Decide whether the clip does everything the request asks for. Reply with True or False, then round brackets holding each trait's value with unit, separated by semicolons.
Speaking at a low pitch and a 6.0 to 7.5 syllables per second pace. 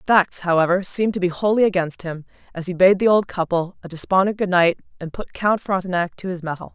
False (185 Hz; 6.2 syllables/s)